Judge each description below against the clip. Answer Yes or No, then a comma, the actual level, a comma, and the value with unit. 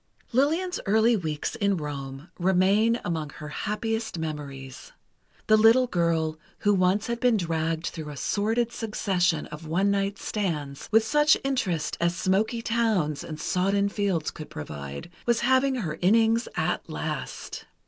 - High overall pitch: Yes, high, 195 Hz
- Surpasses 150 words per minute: No, average, 145 wpm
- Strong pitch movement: Yes, wide, 6.0 semitones